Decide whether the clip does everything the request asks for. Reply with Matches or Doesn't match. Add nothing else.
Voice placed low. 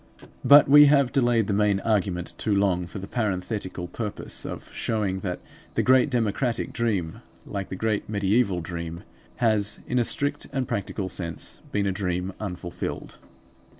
Matches